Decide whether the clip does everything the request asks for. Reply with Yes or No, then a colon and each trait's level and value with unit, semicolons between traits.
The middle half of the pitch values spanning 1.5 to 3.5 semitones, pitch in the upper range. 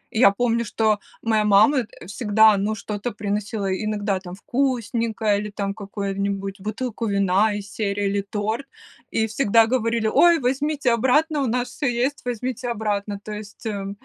Yes: average, 3.0 semitones; high, 215 Hz